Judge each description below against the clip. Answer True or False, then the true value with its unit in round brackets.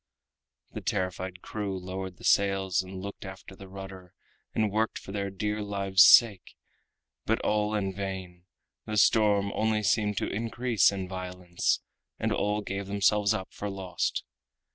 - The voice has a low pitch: True (100 Hz)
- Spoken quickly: False (145 wpm)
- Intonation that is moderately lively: False (1.8 semitones)